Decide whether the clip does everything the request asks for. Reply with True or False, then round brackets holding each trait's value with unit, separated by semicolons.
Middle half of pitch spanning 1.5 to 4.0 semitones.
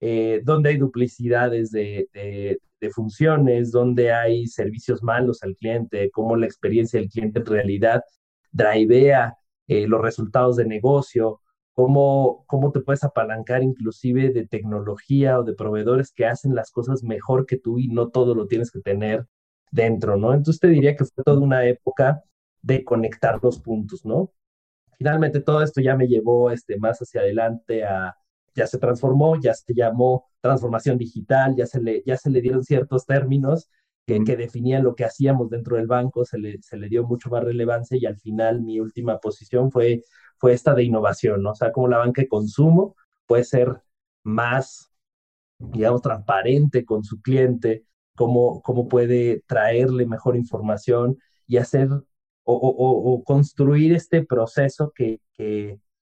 True (2.8 semitones)